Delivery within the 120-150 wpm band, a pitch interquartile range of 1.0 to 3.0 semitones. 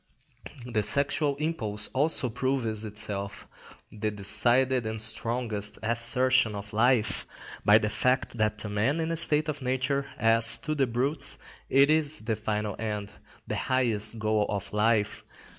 No: average, 145 wpm; average, 3.8 semitones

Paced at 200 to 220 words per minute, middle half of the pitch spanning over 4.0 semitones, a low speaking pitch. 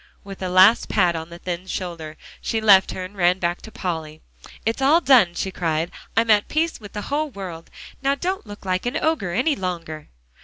No: fast, 205 wpm; average, 4.7 semitones; high, 190 Hz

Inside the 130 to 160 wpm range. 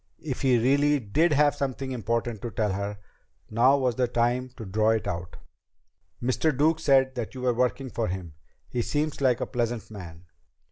No: average, 185 wpm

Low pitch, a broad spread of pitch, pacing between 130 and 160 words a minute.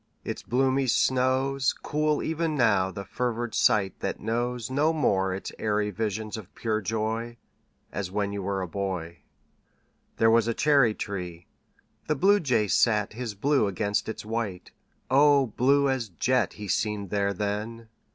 No: low, 110 Hz; average, 4.3 semitones; average, 150 wpm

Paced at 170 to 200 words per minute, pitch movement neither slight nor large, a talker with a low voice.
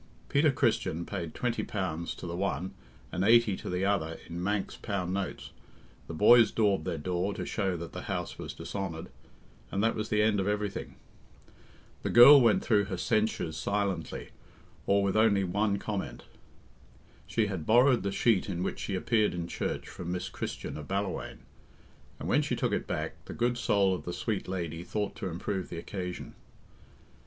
Yes: average, 180 wpm; average, 3.3 semitones; low, 100 Hz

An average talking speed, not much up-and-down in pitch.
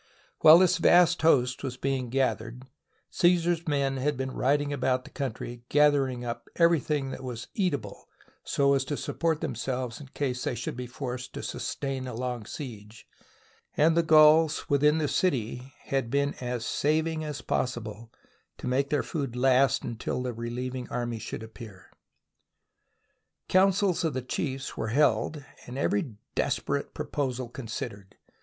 No: average, 150 wpm; average, 3.5 semitones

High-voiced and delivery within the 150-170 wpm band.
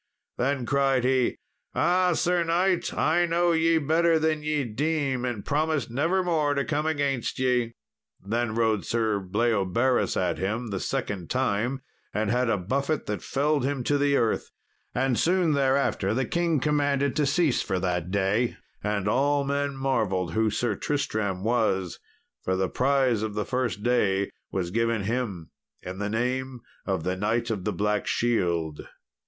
No: low, 125 Hz; average, 160 wpm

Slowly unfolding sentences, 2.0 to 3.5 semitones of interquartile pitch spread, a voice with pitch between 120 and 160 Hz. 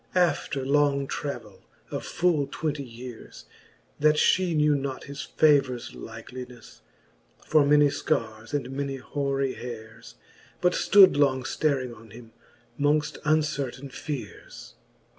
Yes: slow, 120 wpm; average, 3.1 semitones; medium, 140 Hz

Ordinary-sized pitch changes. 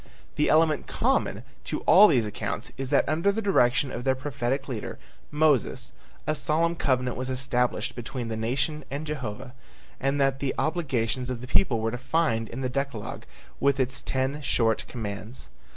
Yes: average, 3.2 semitones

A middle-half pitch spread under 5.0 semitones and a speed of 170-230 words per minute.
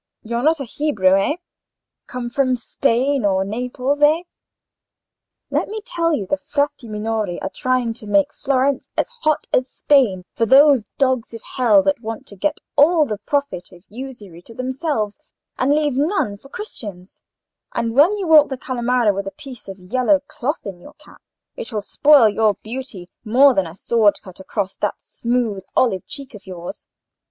No: wide, 5.5 semitones; average, 175 wpm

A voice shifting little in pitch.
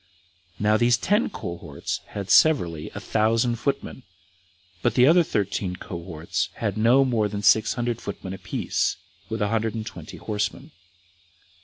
No: average, 3.9 semitones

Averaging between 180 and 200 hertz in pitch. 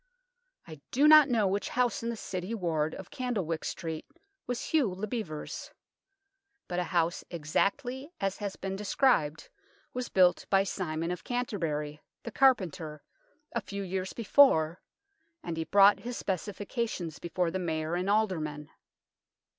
Yes: high, 190 Hz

